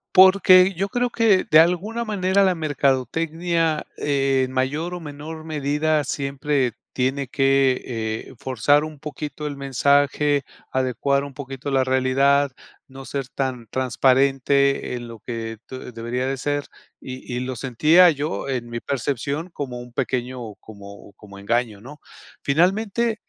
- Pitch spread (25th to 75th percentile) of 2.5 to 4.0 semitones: Yes, average, 3.3 semitones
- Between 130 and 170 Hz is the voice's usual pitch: Yes, medium, 140 Hz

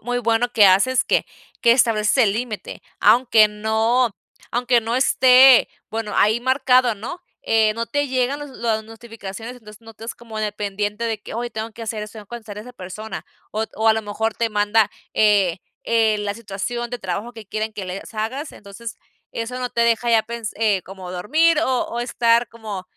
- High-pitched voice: Yes, high, 225 Hz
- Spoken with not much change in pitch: Yes, narrow, 2.3 semitones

